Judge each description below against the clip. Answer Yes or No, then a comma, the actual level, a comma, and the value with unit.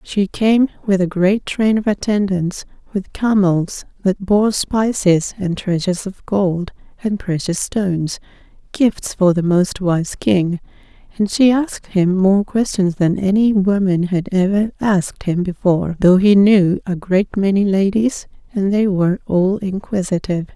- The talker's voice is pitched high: Yes, high, 195 Hz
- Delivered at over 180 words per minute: No, average, 150 wpm